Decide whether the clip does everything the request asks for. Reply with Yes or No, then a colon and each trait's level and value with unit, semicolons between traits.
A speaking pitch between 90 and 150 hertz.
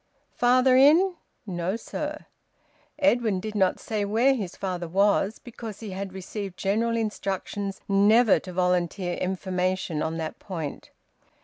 No: high, 200 Hz